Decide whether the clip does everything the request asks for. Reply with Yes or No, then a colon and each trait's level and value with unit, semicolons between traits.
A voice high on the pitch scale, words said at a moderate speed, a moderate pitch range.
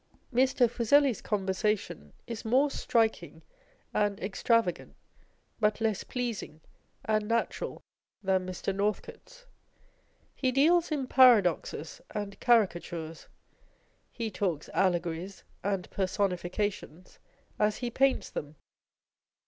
No: high, 210 Hz; slow, 100 wpm; average, 4.5 semitones